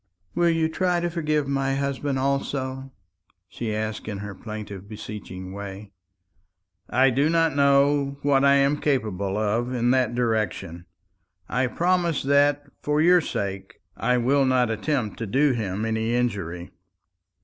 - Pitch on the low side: Yes, low, 130 Hz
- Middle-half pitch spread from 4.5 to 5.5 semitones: Yes, average, 4.9 semitones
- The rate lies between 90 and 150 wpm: Yes, average, 145 wpm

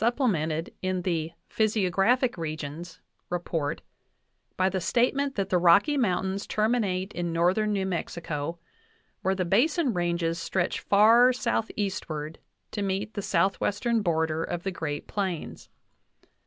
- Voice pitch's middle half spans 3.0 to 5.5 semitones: Yes, average, 4.1 semitones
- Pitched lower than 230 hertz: Yes, medium, 185 Hz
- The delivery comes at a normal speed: No, slow, 125 wpm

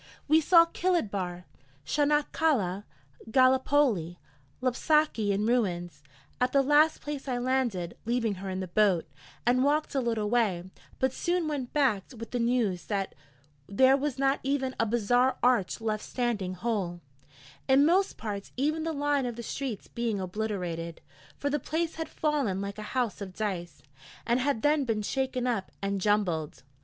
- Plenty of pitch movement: Yes, wide, 5.8 semitones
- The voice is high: Yes, high, 240 Hz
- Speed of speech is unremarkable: Yes, average, 165 wpm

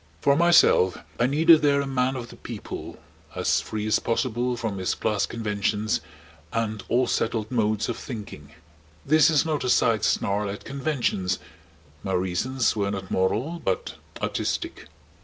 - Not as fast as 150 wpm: No, average, 155 wpm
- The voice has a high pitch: No, low, 115 Hz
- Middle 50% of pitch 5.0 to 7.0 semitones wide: No, average, 4.5 semitones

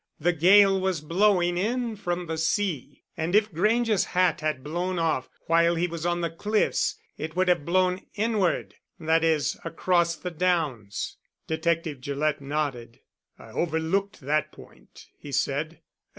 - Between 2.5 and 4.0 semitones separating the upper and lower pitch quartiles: Yes, average, 3.3 semitones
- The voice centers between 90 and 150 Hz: No, medium, 170 Hz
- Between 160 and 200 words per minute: No, average, 150 wpm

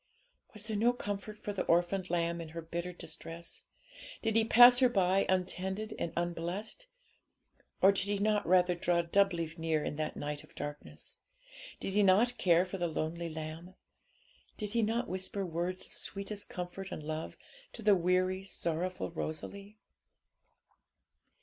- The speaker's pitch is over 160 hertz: Yes, medium, 185 Hz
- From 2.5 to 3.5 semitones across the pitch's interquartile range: Yes, average, 3.2 semitones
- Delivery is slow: No, average, 155 wpm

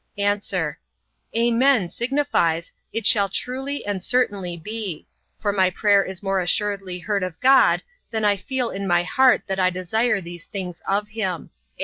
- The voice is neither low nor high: No, high, 200 Hz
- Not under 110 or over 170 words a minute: Yes, average, 155 wpm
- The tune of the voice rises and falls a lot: No, average, 3.8 semitones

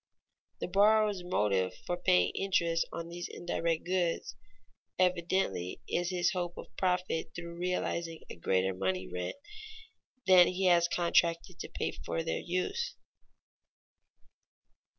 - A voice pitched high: No, medium, 175 Hz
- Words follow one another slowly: Yes, slow, 125 wpm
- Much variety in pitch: No, narrow, 2.5 semitones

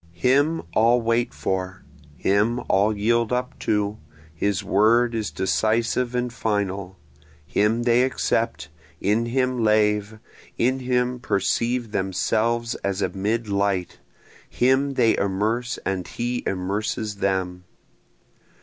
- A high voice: No, low, 110 Hz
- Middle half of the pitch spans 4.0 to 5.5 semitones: No, average, 3.3 semitones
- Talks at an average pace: No, slow, 115 wpm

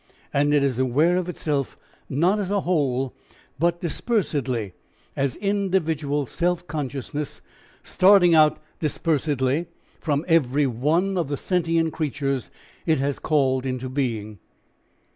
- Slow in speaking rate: Yes, slow, 125 wpm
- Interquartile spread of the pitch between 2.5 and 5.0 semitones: Yes, average, 4.2 semitones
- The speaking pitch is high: No, medium, 150 Hz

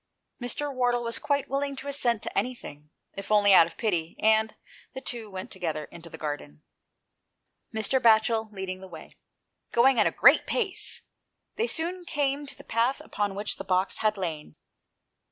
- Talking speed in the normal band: Yes, average, 170 wpm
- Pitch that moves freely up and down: Yes, wide, 6.0 semitones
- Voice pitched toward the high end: Yes, high, 220 Hz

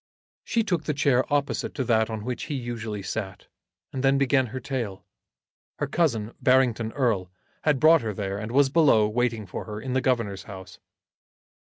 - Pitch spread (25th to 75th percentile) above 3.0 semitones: Yes, average, 4.0 semitones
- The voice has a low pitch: Yes, low, 120 Hz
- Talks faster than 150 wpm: Yes, average, 180 wpm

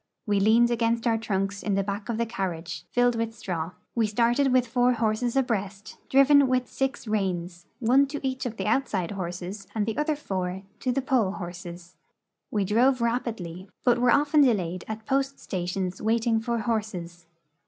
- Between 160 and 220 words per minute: Yes, average, 175 wpm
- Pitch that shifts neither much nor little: Yes, average, 4.5 semitones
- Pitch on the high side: Yes, high, 220 Hz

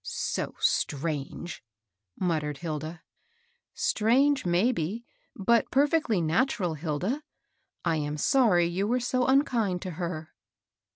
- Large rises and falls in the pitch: Yes, wide, 7.7 semitones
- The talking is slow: Yes, slow, 120 wpm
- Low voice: No, medium, 180 Hz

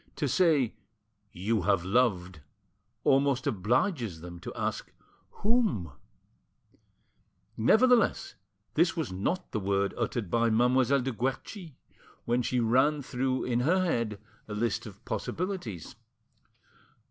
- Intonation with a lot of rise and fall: Yes, wide, 5.7 semitones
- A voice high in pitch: No, low, 120 Hz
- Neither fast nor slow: No, slow, 115 wpm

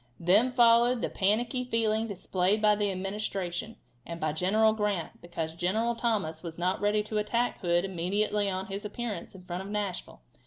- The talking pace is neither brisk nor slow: Yes, average, 170 wpm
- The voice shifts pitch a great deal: No, average, 3.3 semitones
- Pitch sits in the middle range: No, high, 205 Hz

